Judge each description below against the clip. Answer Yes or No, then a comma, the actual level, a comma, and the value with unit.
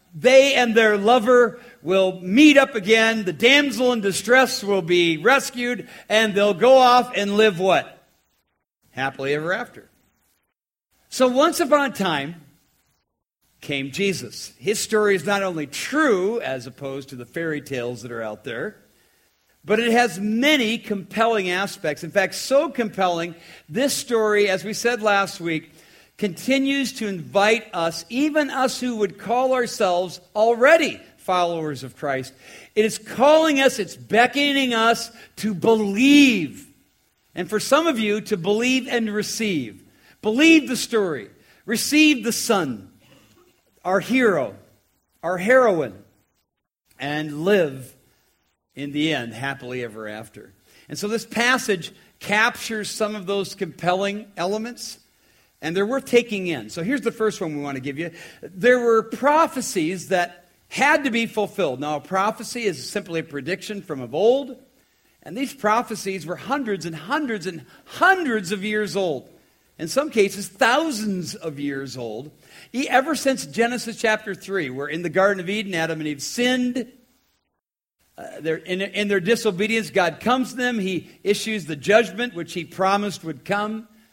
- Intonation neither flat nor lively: No, wide, 6.1 semitones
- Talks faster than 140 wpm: Yes, average, 150 wpm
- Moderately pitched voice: No, high, 205 Hz